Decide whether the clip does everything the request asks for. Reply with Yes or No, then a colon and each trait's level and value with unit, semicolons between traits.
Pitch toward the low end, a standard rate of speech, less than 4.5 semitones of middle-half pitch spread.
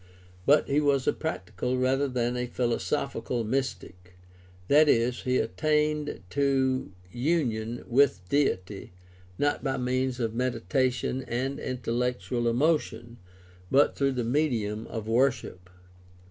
No: low, 125 Hz; slow, 120 wpm; average, 2.9 semitones